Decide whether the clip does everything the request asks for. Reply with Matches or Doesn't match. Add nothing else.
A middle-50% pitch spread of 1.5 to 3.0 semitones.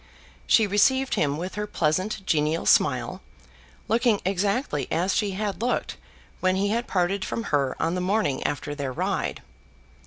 Doesn't match